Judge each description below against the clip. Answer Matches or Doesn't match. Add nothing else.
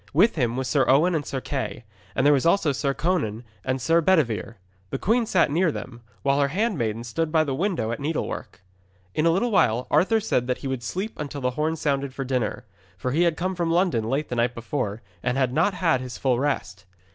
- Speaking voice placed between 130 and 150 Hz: Matches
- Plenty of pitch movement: Doesn't match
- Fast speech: Matches